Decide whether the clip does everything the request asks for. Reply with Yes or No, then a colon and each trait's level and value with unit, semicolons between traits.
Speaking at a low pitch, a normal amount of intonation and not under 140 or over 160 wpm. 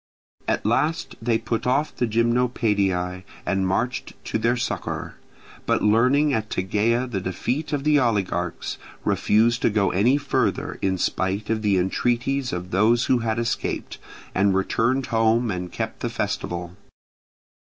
Yes: low, 115 Hz; average, 4.2 semitones; average, 145 wpm